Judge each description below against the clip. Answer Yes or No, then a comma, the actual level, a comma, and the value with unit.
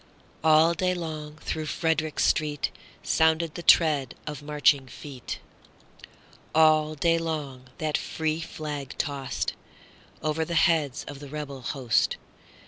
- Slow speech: Yes, slow, 110 wpm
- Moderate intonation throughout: No, narrow, 1.9 semitones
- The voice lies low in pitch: No, medium, 155 Hz